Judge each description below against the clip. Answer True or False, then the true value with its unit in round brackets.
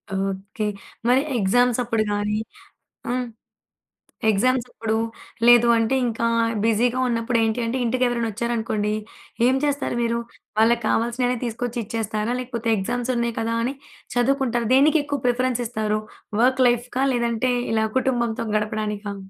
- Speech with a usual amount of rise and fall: False (2.1 semitones)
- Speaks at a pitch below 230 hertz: False (235 Hz)